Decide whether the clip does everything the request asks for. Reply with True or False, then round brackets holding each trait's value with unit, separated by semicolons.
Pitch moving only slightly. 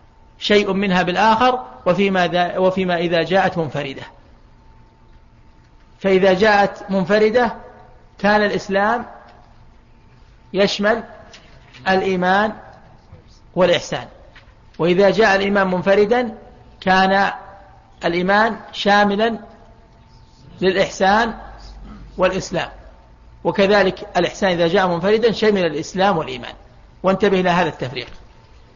False (3.9 semitones)